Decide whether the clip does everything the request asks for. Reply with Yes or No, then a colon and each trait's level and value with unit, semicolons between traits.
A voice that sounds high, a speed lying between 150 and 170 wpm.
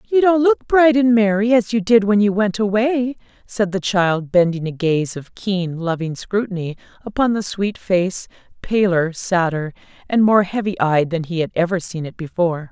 No: high, 195 Hz; average, 190 wpm